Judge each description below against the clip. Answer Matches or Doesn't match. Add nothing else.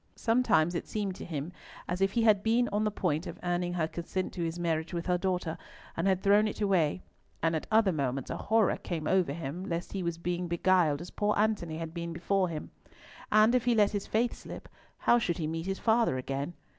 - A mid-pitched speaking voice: Matches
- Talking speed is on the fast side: Matches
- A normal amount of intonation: Matches